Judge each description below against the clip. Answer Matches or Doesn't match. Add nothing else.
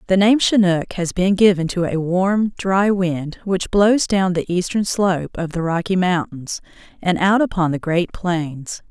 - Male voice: Doesn't match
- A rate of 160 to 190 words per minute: Matches